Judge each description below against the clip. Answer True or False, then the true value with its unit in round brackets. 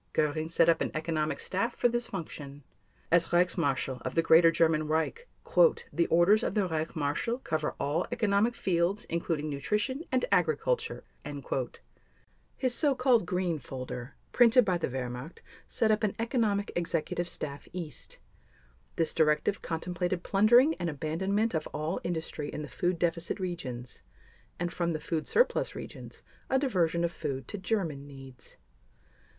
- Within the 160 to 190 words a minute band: False (150 wpm)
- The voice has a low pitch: False (170 Hz)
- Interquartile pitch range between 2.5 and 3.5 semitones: False (5.0 semitones)